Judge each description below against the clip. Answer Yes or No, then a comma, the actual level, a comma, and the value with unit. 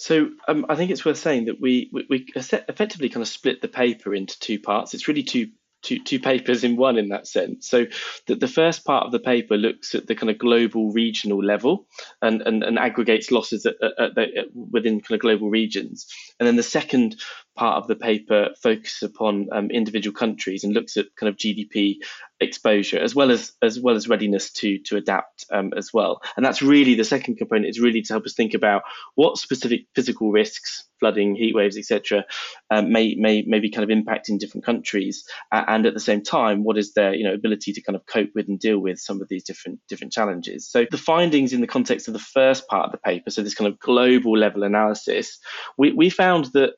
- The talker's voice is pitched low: Yes, low, 110 Hz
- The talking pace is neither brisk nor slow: No, fast, 225 wpm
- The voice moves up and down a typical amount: Yes, average, 3.4 semitones